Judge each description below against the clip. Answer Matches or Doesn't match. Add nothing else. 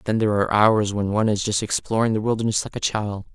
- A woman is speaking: Doesn't match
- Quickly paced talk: Matches